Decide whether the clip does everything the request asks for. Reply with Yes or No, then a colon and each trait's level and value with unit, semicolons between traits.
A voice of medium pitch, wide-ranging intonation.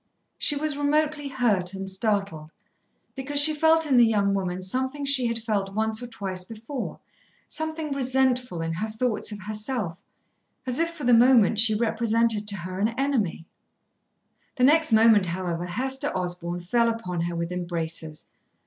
No: high, 225 Hz; wide, 6.0 semitones